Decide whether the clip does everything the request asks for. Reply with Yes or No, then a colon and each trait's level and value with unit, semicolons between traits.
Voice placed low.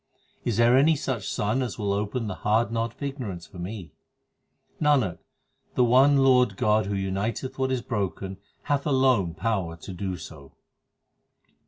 Yes: low, 110 Hz